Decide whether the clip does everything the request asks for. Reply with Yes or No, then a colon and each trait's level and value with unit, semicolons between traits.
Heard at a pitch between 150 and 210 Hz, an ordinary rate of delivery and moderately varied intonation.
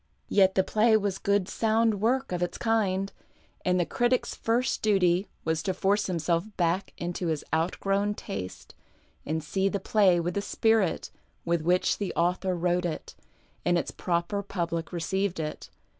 Yes: medium, 185 Hz; average, 160 wpm; average, 3.0 semitones